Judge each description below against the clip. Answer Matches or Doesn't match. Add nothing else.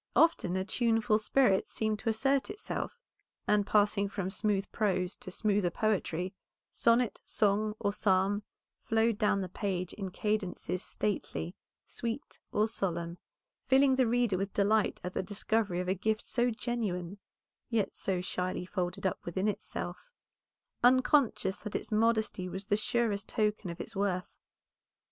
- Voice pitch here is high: Matches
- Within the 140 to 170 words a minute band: Matches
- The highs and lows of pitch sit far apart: Doesn't match